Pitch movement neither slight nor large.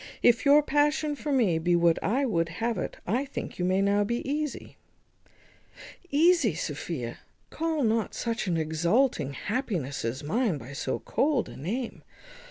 No: wide, 8.6 semitones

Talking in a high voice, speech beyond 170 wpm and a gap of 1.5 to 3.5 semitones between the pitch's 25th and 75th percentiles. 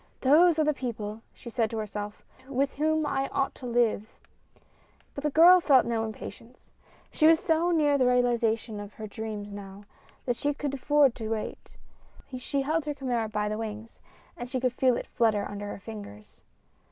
No: high, 245 Hz; average, 185 wpm; average, 4.6 semitones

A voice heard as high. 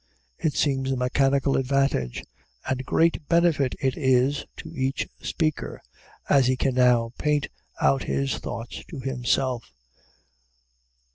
No: low, 135 Hz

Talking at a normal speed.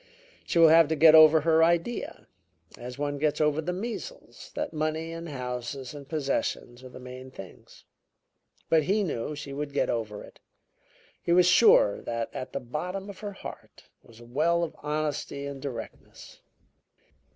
Yes: average, 170 wpm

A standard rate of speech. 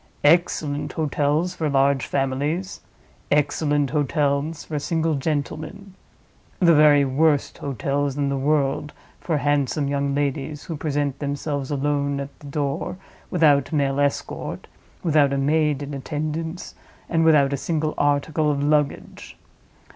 No: slow, 130 wpm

